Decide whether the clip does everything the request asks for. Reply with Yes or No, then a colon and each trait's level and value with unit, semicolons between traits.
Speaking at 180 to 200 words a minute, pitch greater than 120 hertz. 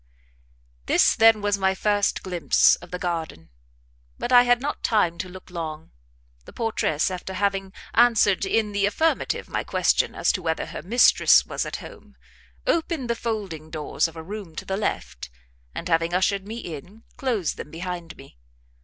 No: average, 170 wpm; high, 190 Hz